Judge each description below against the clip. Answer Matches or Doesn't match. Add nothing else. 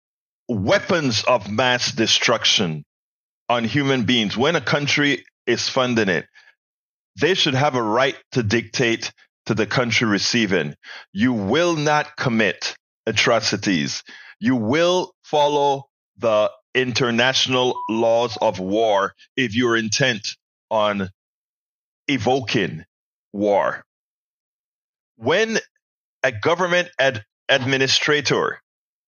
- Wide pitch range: Doesn't match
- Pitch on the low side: Matches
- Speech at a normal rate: Doesn't match